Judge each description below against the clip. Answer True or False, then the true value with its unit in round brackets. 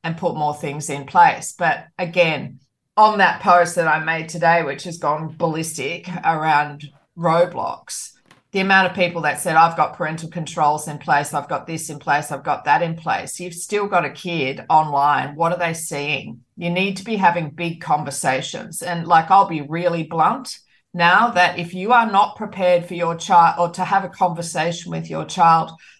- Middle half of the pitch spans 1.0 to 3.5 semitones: True (2.7 semitones)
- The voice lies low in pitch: False (170 Hz)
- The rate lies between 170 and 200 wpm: True (195 wpm)